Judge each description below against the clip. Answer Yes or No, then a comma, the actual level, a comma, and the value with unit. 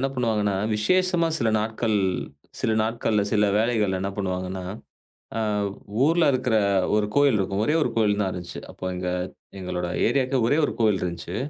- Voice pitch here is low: Yes, low, 105 Hz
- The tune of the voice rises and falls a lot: No, average, 4.4 semitones